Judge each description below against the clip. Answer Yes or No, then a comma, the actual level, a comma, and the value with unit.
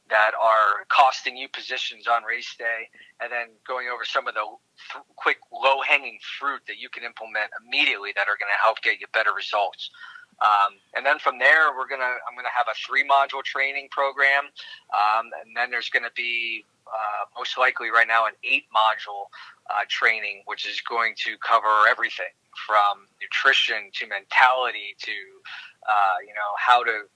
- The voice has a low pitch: Yes, low, 125 Hz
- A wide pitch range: No, average, 4.1 semitones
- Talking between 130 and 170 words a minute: No, average, 185 wpm